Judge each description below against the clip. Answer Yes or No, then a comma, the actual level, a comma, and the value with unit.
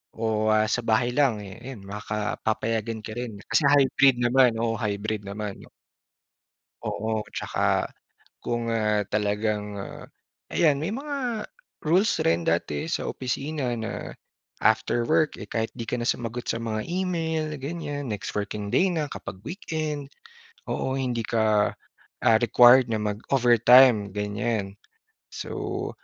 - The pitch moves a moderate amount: Yes, average, 4.3 semitones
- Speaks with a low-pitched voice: Yes, low, 115 Hz